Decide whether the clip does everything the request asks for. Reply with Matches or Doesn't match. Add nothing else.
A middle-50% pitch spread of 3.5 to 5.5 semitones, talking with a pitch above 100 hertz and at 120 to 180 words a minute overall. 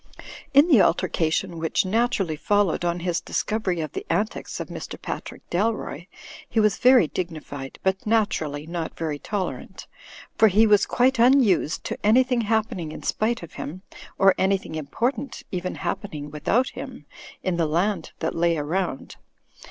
Matches